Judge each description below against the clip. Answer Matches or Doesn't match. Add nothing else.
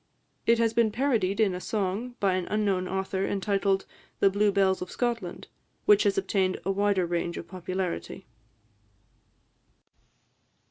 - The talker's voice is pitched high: Matches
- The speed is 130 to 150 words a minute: Matches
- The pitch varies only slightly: Matches